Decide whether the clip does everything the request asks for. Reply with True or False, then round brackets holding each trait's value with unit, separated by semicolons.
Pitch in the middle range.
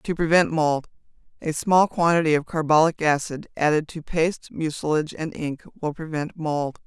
True (155 Hz)